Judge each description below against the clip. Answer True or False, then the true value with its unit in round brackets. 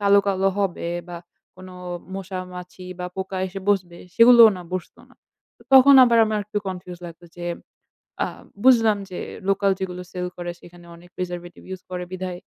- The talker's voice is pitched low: False (185 Hz)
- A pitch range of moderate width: False (2.1 semitones)